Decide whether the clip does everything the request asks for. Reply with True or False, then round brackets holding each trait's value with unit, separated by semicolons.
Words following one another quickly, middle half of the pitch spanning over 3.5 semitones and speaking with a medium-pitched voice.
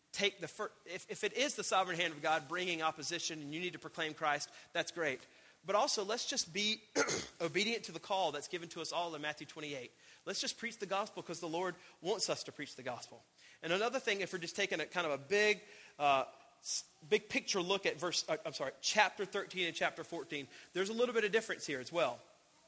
True (235 wpm; 4.5 semitones; 180 Hz)